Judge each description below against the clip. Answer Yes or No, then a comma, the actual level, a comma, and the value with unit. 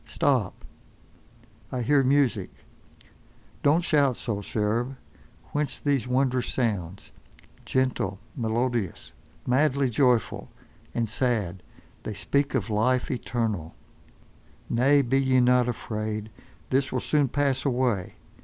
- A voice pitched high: No, low, 125 Hz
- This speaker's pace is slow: Yes, slow, 105 wpm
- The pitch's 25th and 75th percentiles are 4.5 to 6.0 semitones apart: No, average, 3.6 semitones